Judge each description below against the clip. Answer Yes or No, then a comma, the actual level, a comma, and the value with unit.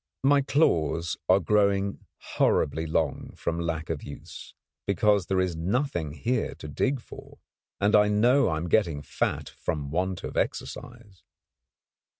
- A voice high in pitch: No, very low, 95 Hz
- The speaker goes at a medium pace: Yes, average, 145 wpm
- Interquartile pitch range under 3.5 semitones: No, average, 4.6 semitones